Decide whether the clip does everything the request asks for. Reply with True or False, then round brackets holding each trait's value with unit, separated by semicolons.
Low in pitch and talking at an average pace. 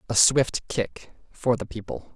True (115 Hz; 165 wpm)